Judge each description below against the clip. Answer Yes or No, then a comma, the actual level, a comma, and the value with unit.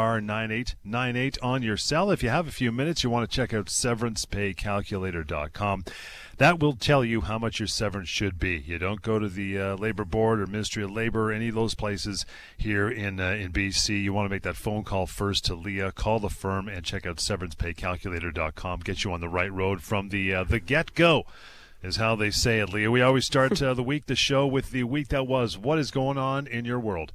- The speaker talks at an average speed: No, fast, 235 wpm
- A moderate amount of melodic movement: Yes, average, 4.1 semitones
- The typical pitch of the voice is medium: No, low, 105 Hz